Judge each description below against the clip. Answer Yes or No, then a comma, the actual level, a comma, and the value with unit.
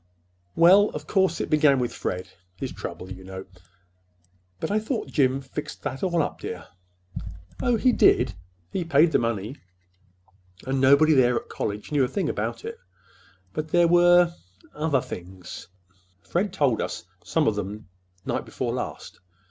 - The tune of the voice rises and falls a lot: Yes, wide, 8.4 semitones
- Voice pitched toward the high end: No, medium, 140 Hz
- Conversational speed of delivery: Yes, average, 150 wpm